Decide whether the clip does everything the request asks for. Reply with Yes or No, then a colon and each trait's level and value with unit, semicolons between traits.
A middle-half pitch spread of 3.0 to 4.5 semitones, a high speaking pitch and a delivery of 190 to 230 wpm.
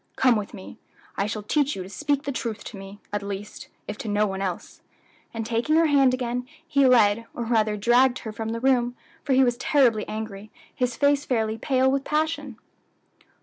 Yes: average, 4.0 semitones; high, 235 Hz; average, 200 wpm